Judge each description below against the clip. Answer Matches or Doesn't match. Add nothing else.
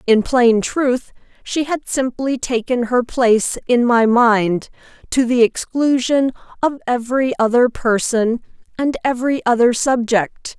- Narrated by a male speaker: Doesn't match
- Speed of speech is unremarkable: Doesn't match